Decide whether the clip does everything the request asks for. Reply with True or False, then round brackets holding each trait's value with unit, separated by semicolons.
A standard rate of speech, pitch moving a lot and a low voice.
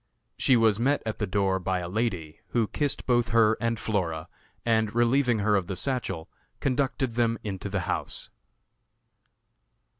False (155 wpm; 3.8 semitones; 110 Hz)